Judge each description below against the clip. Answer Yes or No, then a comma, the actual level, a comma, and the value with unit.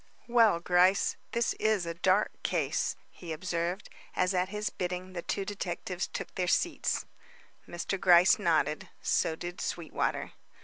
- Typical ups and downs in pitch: No, narrow, 2.2 semitones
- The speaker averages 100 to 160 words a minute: Yes, average, 140 wpm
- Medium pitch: Yes, medium, 180 Hz